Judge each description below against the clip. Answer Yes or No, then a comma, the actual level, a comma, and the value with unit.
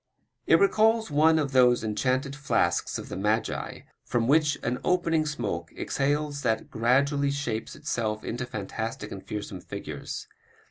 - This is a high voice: No, low, 130 Hz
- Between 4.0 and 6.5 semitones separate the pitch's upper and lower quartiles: Yes, average, 4.9 semitones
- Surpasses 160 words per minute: No, average, 140 wpm